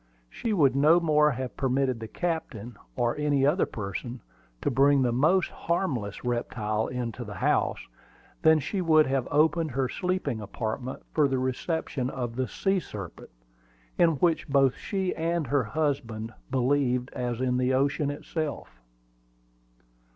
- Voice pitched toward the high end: No, low, 135 Hz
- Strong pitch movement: No, average, 4.3 semitones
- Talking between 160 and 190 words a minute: No, average, 145 wpm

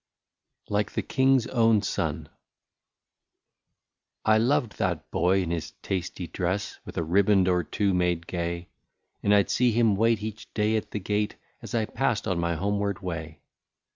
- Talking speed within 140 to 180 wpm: Yes, average, 170 wpm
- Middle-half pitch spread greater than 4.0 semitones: No, average, 3.7 semitones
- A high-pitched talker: No, low, 100 Hz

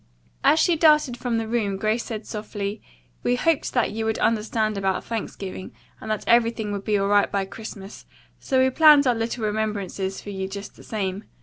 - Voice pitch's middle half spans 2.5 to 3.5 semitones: Yes, average, 2.9 semitones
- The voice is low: No, high, 215 Hz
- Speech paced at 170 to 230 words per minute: Yes, average, 195 wpm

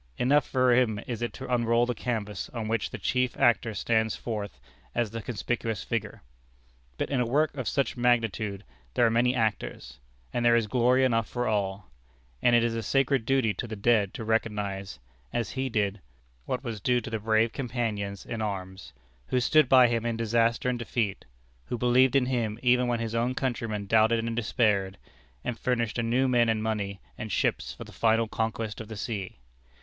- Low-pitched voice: Yes, low, 115 Hz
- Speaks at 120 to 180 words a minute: No, average, 195 wpm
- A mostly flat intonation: Yes, narrow, 2.3 semitones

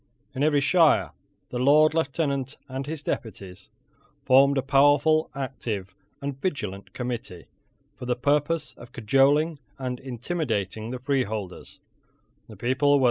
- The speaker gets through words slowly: Yes, slow, 115 wpm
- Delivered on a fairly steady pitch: No, average, 3.5 semitones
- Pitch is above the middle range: No, low, 135 Hz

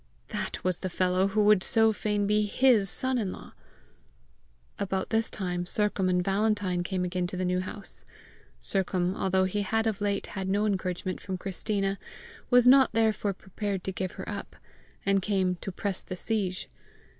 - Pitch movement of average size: No, narrow, 2.3 semitones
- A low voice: No, high, 195 Hz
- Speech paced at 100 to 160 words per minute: No, average, 175 wpm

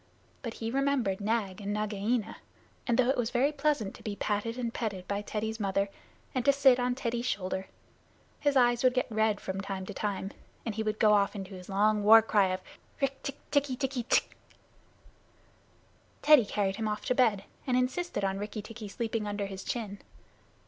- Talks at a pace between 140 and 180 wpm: No, average, 190 wpm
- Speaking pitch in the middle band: No, high, 220 Hz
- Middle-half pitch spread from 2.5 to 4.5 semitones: Yes, average, 3.6 semitones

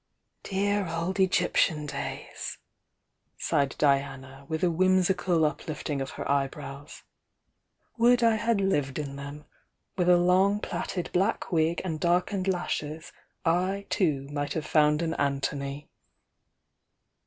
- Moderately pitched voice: Yes, medium, 165 Hz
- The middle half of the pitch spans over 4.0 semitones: Yes, average, 4.6 semitones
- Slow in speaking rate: Yes, slow, 125 wpm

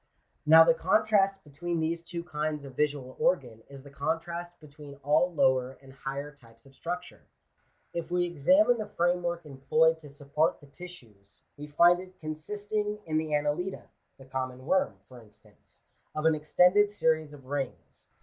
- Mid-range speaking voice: Yes, medium, 155 Hz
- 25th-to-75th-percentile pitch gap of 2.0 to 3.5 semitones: No, average, 3.9 semitones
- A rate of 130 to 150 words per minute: No, average, 165 wpm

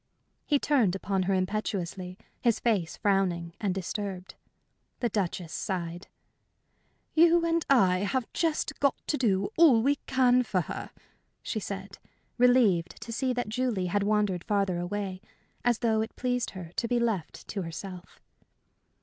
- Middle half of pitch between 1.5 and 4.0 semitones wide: No, average, 4.9 semitones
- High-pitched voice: Yes, high, 205 Hz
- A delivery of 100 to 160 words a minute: Yes, average, 150 wpm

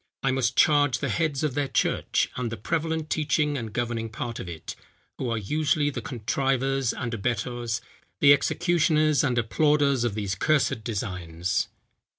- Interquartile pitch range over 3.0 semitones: Yes, average, 4.3 semitones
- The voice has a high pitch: No, low, 130 Hz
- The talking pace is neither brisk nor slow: Yes, average, 160 wpm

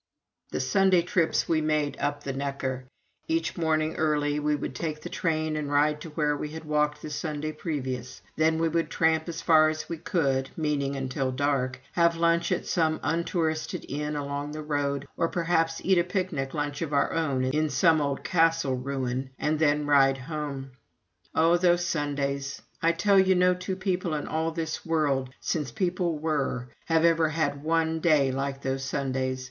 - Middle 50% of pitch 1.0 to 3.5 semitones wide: Yes, average, 2.8 semitones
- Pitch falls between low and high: Yes, medium, 155 Hz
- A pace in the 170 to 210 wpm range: Yes, average, 180 wpm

